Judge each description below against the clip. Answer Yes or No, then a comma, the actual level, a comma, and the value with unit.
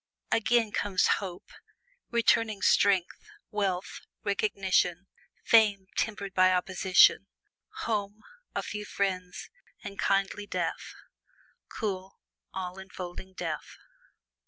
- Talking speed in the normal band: No, slow, 90 wpm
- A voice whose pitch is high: Yes, high, 195 Hz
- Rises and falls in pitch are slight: Yes, narrow, 2.0 semitones